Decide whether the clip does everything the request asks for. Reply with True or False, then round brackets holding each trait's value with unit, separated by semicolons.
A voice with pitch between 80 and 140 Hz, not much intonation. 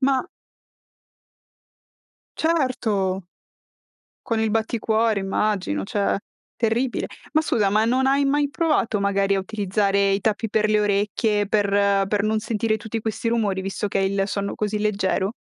False (210 Hz; 2.3 semitones)